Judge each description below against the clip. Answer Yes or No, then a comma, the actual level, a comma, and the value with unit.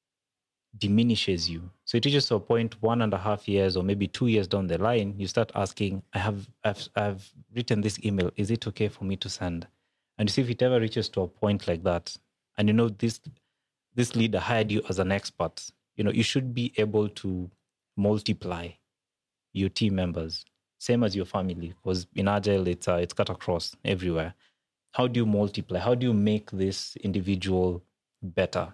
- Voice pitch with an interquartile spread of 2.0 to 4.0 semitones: Yes, average, 3.3 semitones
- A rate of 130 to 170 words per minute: No, average, 200 wpm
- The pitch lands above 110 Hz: No, low, 100 Hz